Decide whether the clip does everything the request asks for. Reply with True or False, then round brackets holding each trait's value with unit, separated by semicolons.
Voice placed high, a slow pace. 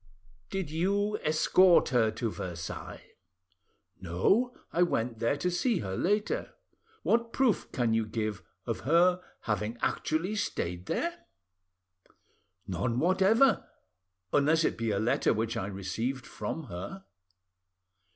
False (140 Hz; 120 wpm)